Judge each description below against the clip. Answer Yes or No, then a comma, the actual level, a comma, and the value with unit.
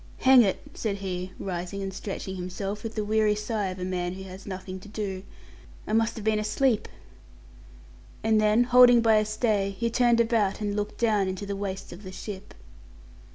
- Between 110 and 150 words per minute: No, average, 195 wpm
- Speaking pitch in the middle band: No, high, 205 Hz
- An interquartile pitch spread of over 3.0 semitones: No, narrow, 2.5 semitones